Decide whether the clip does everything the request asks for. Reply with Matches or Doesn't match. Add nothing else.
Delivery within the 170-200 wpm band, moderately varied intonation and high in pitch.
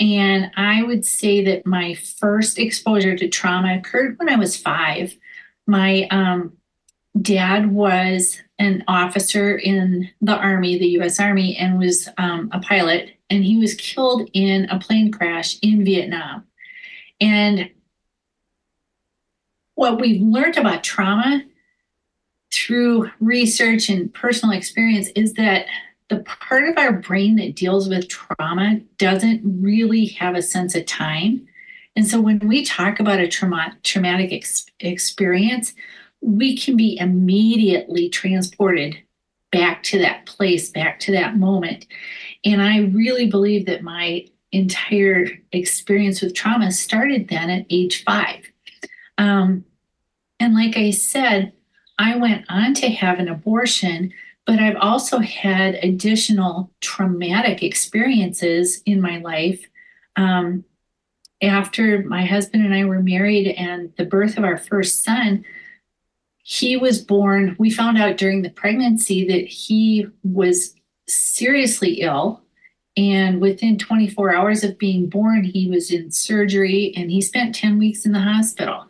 Doesn't match